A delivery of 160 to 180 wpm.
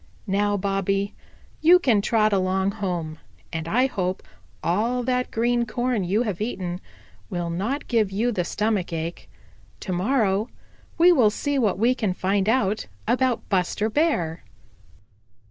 No: average, 145 wpm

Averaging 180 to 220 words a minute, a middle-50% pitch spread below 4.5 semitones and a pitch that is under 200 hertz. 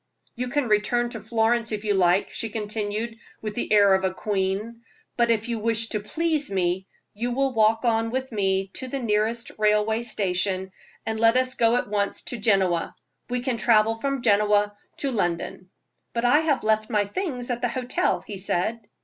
No: average, 190 wpm; average, 2.7 semitones; high, 220 Hz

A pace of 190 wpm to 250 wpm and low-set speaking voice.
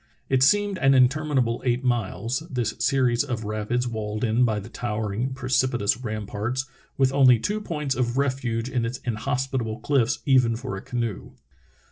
No: average, 160 wpm; low, 125 Hz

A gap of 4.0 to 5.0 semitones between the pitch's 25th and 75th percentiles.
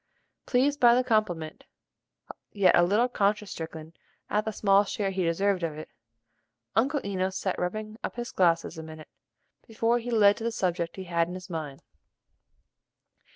Yes: average, 4.7 semitones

